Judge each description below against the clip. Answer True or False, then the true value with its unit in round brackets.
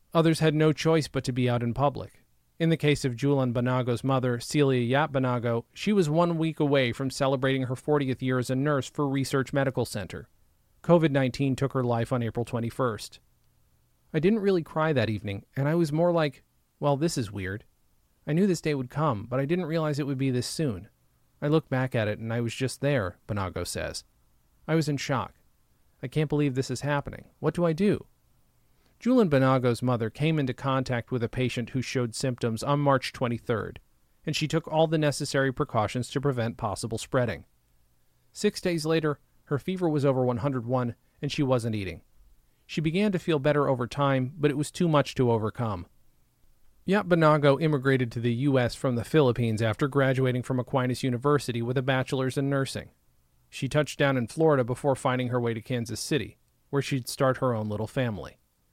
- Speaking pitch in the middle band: False (130 Hz)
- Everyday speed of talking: True (195 wpm)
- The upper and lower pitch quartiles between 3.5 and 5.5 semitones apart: True (3.8 semitones)